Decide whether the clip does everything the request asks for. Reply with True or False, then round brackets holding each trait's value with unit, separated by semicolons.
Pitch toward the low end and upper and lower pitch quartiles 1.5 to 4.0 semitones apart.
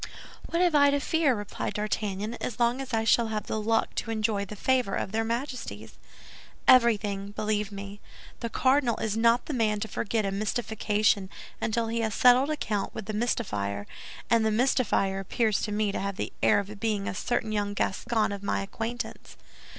False (220 Hz; 2.7 semitones)